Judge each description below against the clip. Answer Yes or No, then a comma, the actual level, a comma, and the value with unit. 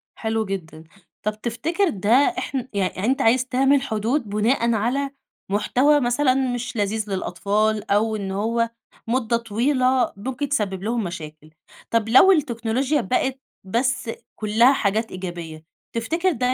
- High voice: Yes, high, 230 Hz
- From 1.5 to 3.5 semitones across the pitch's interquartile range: No, average, 4.1 semitones